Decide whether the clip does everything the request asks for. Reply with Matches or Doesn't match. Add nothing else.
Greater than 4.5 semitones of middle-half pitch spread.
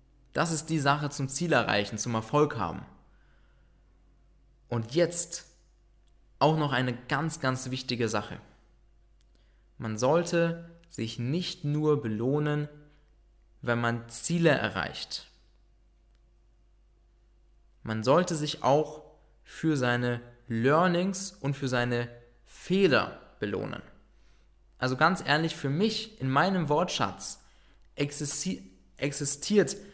Matches